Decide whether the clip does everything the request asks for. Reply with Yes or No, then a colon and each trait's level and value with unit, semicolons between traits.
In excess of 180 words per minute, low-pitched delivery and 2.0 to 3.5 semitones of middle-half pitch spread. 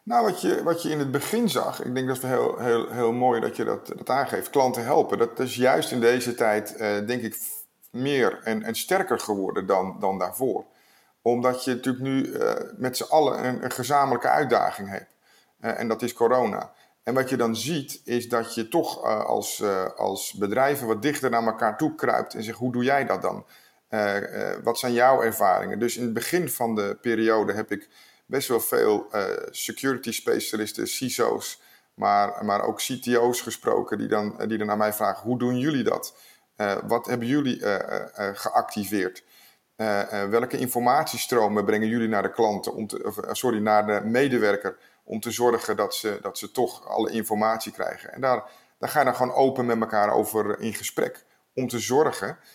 Yes: average, 195 wpm; low, 120 Hz; average, 2.8 semitones